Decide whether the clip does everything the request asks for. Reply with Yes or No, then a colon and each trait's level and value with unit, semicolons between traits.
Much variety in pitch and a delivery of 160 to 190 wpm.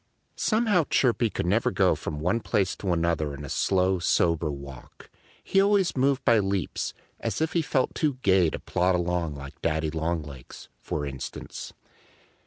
Yes: wide, 8.0 semitones; average, 165 wpm